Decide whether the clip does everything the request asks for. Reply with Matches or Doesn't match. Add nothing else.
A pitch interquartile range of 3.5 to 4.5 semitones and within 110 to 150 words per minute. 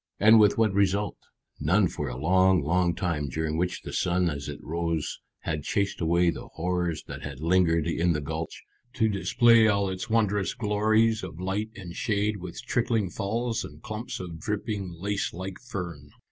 Doesn't match